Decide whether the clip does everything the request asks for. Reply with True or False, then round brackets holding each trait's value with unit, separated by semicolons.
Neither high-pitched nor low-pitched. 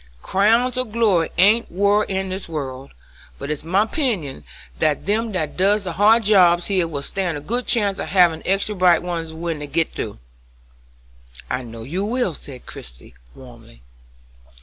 True (180 Hz)